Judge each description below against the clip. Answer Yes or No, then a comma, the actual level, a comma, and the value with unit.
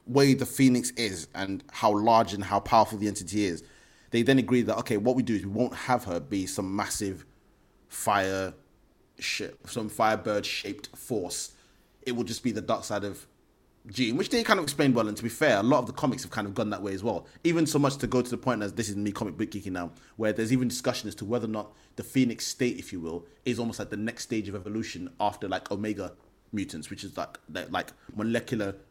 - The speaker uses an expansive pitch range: No, average, 3.3 semitones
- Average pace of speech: No, fast, 240 wpm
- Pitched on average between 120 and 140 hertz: No, low, 110 Hz